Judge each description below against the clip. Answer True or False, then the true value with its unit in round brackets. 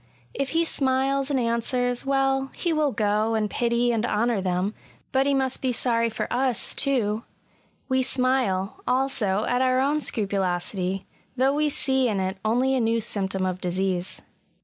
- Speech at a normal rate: True (170 wpm)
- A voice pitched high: True (240 Hz)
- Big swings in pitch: False (4.5 semitones)